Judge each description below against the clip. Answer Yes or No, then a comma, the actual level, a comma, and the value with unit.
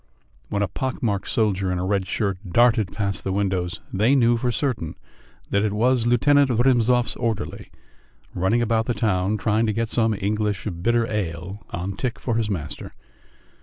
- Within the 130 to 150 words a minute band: No, average, 170 wpm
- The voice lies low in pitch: Yes, low, 110 Hz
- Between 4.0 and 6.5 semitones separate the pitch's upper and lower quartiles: No, average, 3.3 semitones